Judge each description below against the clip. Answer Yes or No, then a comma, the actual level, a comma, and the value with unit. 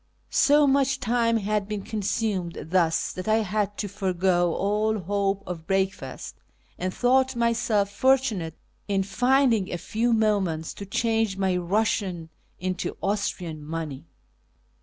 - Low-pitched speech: No, high, 200 Hz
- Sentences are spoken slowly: Yes, slow, 130 wpm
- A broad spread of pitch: No, average, 3.4 semitones